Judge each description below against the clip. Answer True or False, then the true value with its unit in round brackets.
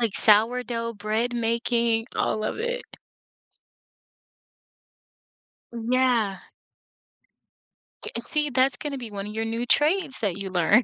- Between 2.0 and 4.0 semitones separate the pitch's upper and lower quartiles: True (2.9 semitones)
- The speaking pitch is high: True (235 Hz)